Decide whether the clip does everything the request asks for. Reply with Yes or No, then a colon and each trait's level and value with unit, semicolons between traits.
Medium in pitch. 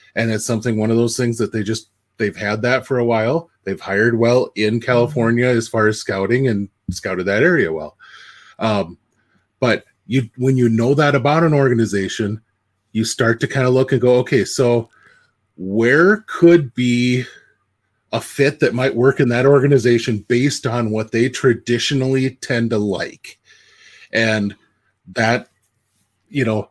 No: low, 120 Hz